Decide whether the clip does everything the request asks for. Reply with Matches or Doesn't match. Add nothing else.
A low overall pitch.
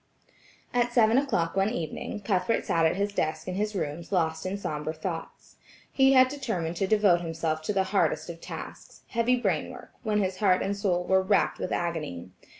Doesn't match